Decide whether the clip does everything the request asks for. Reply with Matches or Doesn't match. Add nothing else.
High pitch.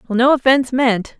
Matches